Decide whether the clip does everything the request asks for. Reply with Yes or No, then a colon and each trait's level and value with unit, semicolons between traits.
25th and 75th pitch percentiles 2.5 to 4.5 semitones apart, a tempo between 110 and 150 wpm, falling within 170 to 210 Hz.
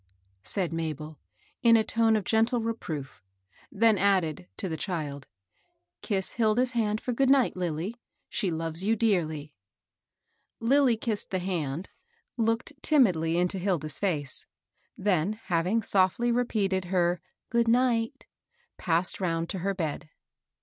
No: wide, 5.5 semitones; average, 145 wpm; high, 190 Hz